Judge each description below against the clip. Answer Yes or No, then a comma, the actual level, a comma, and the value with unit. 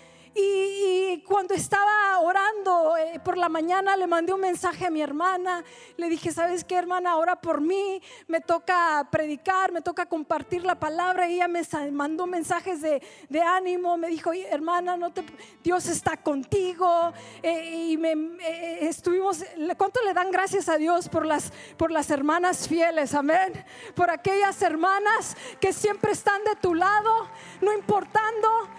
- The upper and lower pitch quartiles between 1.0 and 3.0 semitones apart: Yes, narrow, 2.6 semitones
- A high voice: Yes, very high, 355 Hz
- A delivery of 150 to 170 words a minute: Yes, average, 160 wpm